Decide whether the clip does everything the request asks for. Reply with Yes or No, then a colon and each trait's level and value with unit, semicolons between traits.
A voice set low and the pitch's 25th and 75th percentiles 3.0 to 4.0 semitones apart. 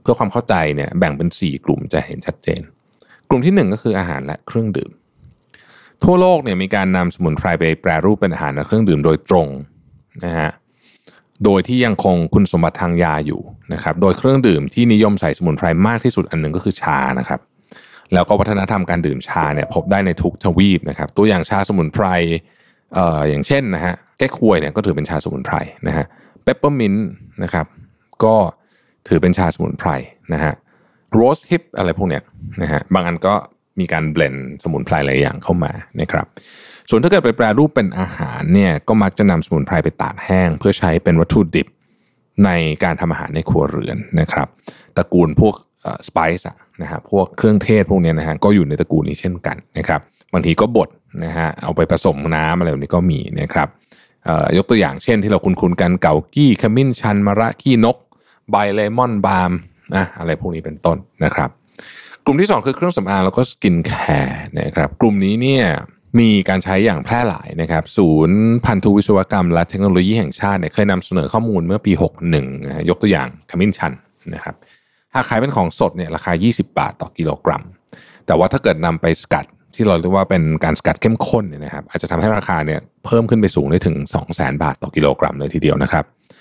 No: very low, 95 Hz; average, 4.5 semitones